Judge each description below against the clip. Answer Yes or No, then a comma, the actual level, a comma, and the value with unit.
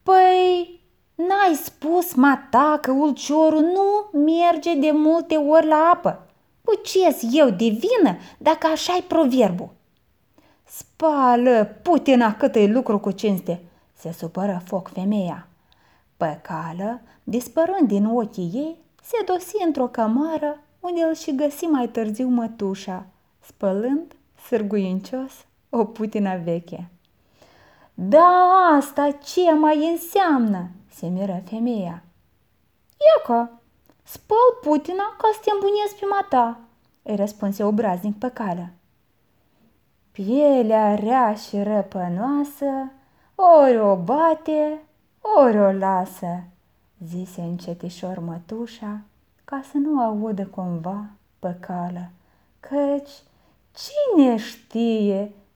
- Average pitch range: No, wide, 7.7 semitones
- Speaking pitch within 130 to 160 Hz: No, high, 245 Hz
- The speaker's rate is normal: No, slow, 105 wpm